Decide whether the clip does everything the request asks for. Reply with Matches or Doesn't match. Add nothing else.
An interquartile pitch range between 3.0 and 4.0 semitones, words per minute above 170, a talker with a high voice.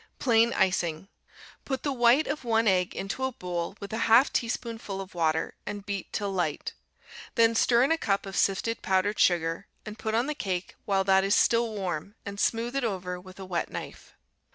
Matches